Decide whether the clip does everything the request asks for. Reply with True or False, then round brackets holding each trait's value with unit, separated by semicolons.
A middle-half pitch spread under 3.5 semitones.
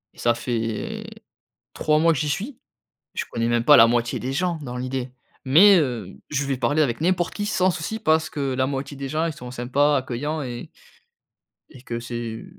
False (4.4 semitones)